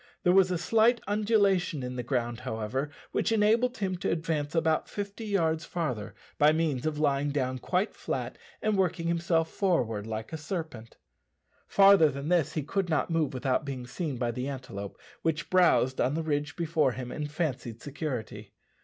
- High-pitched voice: No, medium, 155 Hz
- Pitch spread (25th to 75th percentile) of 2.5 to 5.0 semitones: No, wide, 5.6 semitones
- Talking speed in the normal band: Yes, average, 175 wpm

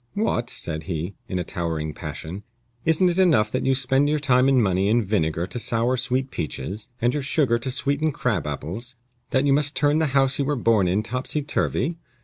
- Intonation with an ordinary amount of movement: No, wide, 6.7 semitones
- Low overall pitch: Yes, low, 125 Hz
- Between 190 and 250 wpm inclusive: Yes, fast, 205 wpm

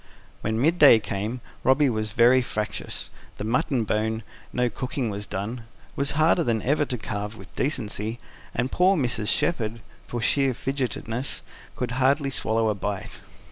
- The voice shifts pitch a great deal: No, average, 3.7 semitones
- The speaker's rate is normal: Yes, average, 150 wpm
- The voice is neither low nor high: No, low, 120 Hz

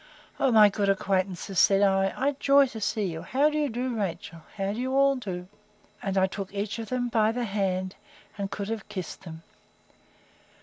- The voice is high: Yes, high, 205 Hz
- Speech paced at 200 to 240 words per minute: Yes, fast, 205 wpm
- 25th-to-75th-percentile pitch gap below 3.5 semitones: No, average, 4.0 semitones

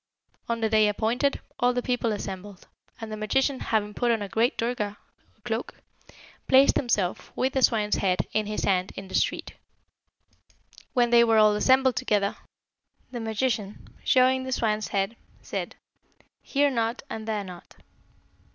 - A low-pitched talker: No, high, 225 Hz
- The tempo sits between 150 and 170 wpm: Yes, average, 155 wpm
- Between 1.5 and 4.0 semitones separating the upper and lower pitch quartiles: Yes, average, 3.1 semitones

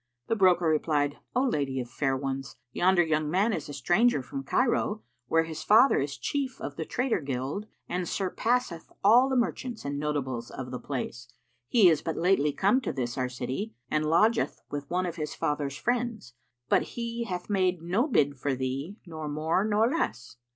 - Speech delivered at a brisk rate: No, average, 185 wpm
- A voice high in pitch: No, medium, 165 Hz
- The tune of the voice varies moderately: No, wide, 7.4 semitones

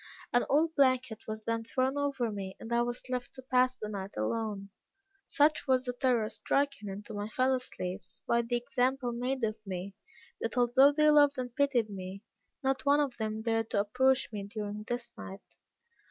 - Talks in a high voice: Yes, high, 240 Hz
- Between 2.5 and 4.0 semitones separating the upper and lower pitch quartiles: Yes, average, 3.7 semitones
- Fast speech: No, average, 185 wpm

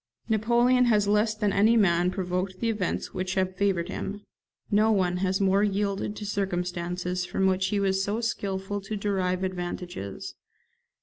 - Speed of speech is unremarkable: Yes, average, 160 wpm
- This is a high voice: Yes, high, 195 Hz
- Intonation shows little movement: Yes, narrow, 2.2 semitones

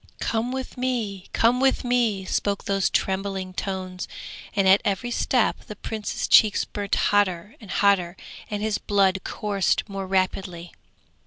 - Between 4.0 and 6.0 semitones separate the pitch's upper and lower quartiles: No, narrow, 2.5 semitones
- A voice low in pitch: No, high, 200 Hz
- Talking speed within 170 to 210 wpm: No, average, 145 wpm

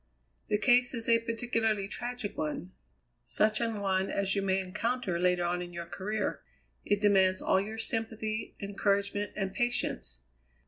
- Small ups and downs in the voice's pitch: No, average, 3.0 semitones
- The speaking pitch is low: No, high, 205 Hz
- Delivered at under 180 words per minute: Yes, average, 150 wpm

